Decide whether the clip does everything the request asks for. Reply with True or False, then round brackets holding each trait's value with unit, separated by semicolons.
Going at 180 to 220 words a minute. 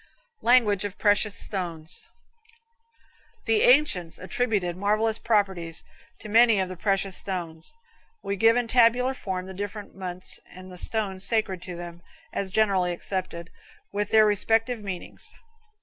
False (135 wpm)